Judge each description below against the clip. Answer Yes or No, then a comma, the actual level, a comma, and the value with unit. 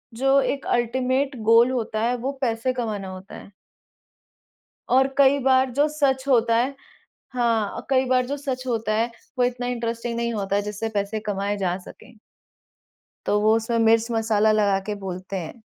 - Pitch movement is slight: No, average, 3.2 semitones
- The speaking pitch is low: No, high, 235 Hz